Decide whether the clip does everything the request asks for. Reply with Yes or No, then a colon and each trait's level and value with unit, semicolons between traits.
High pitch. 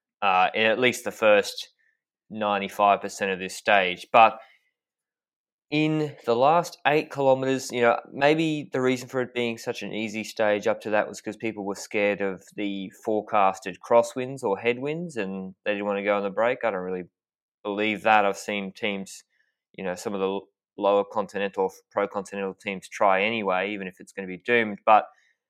No: low, 105 Hz